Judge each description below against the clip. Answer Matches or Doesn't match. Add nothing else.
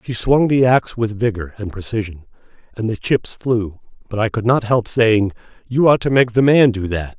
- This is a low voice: Matches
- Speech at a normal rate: Doesn't match